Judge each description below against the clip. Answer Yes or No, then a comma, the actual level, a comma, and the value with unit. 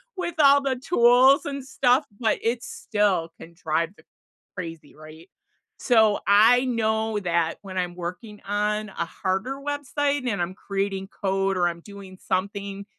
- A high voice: Yes, high, 205 Hz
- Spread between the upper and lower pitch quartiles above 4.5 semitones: Yes, average, 5.1 semitones